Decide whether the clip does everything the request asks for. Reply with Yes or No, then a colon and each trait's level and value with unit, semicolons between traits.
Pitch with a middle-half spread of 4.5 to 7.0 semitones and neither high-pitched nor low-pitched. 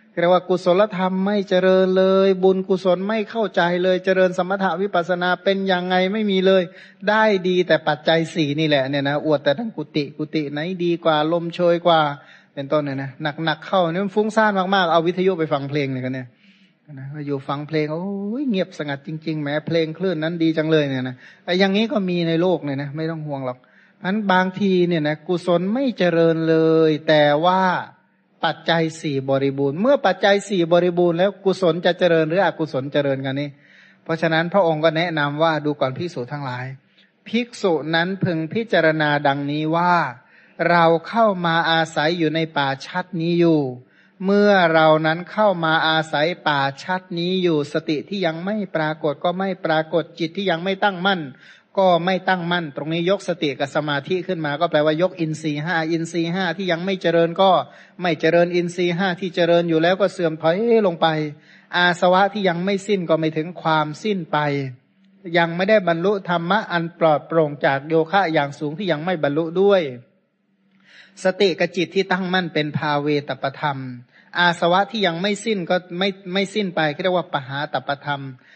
No: average, 3.5 semitones; medium, 170 Hz